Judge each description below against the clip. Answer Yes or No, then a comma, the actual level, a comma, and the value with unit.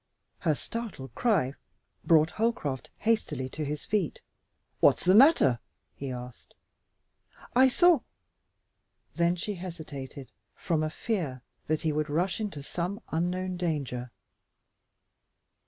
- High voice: No, medium, 165 Hz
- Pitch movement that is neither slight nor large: No, wide, 6.0 semitones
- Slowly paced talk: Yes, slow, 120 wpm